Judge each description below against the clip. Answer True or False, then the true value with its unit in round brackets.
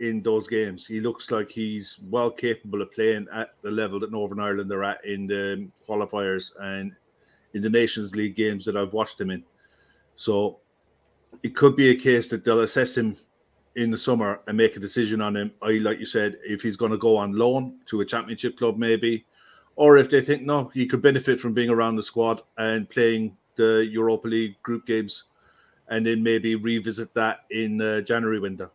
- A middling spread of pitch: False (1.8 semitones)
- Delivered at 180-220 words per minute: True (200 wpm)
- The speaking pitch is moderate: False (110 Hz)